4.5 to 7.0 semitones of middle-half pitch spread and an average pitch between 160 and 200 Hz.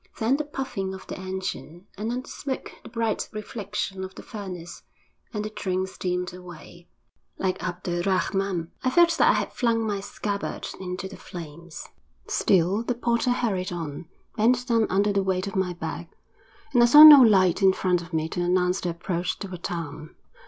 No: average, 3.8 semitones; high, 190 Hz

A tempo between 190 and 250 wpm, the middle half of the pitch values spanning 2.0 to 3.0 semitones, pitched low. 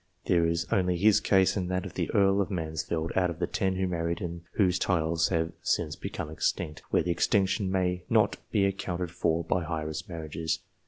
Yes: average, 200 wpm; narrow, 2.4 semitones; very low, 90 Hz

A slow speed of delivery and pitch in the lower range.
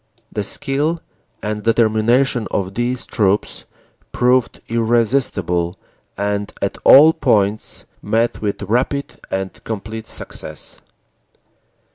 Yes: slow, 95 wpm; low, 110 Hz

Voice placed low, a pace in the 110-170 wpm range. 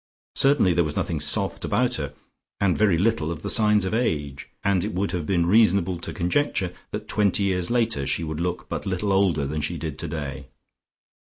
No: very low, 90 Hz; average, 195 wpm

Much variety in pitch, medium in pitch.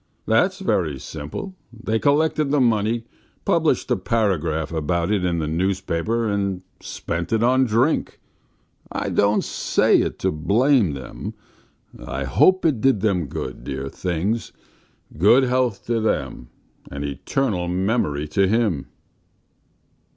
No: wide, 6.4 semitones; low, 100 Hz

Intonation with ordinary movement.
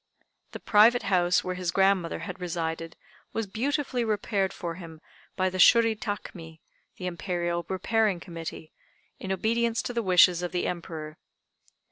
Yes: average, 3.9 semitones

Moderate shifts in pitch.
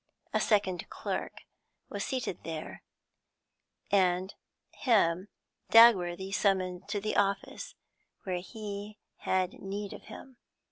No: narrow, 2.3 semitones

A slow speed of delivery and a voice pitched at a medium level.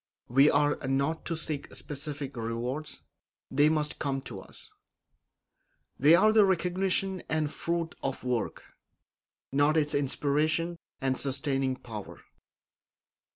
Yes: slow, 115 wpm; medium, 145 Hz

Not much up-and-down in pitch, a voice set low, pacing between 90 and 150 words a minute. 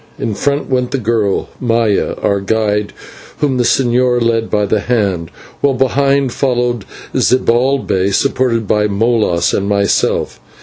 No: average, 3.8 semitones; low, 115 Hz; slow, 135 wpm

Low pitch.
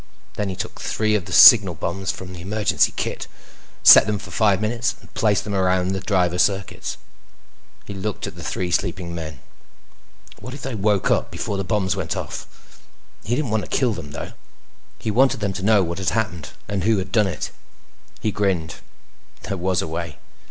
Yes: low, 100 Hz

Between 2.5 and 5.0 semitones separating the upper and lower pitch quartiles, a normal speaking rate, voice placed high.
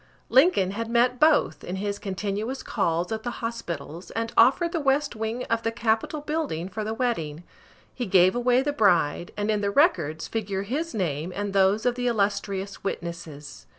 Yes: average, 4.6 semitones; average, 180 wpm; high, 215 Hz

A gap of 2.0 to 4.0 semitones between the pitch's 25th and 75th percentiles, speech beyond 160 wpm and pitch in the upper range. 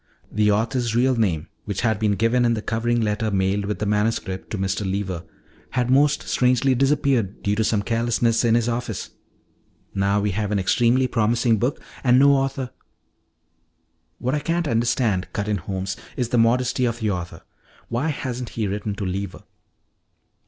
No: average, 3.4 semitones; average, 175 wpm; low, 115 Hz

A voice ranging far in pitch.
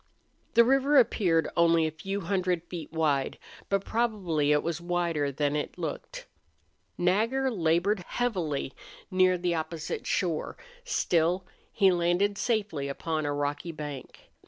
No: average, 4.0 semitones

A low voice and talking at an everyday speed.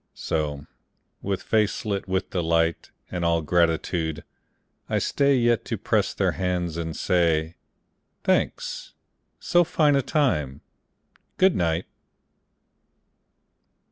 No: very low, 85 Hz; slow, 110 wpm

